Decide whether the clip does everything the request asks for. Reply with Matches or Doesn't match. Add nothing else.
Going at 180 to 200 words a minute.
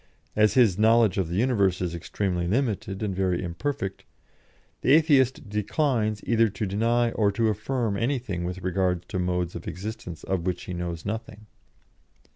Doesn't match